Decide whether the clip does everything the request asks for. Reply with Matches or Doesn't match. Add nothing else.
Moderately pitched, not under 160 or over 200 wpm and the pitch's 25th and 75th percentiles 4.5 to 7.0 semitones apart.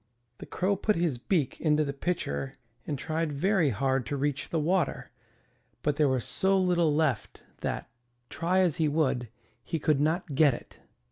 Doesn't match